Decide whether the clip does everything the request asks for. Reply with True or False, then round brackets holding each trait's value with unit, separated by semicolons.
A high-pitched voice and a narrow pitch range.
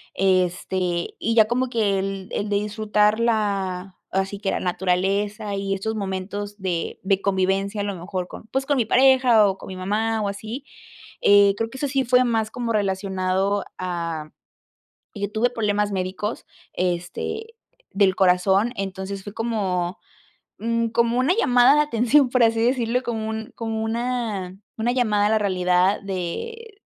False (205 Hz; 3.3 semitones)